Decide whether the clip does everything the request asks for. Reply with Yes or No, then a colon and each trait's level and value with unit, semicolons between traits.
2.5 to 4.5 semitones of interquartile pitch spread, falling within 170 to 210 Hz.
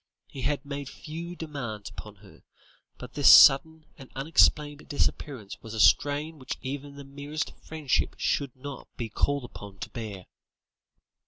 No: average, 3.6 semitones; medium, 140 Hz